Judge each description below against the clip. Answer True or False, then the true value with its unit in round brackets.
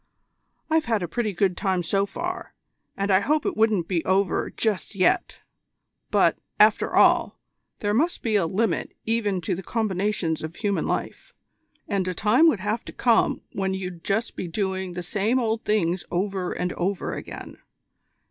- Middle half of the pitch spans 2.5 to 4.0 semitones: True (3.2 semitones)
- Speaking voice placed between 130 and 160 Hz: False (200 Hz)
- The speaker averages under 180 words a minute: True (170 wpm)